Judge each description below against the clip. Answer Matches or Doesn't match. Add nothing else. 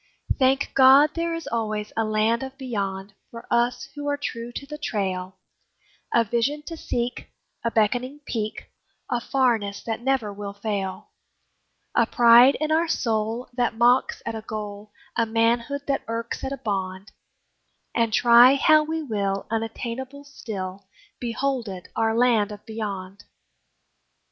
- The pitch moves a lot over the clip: Doesn't match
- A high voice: Matches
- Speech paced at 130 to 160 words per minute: Matches